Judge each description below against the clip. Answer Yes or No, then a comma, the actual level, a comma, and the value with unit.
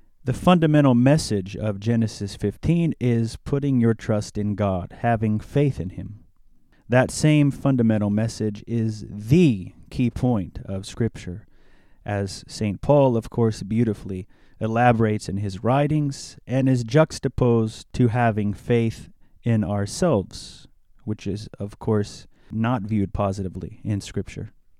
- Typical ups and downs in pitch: Yes, average, 3.6 semitones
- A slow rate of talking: Yes, slow, 130 wpm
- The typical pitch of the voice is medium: No, low, 110 Hz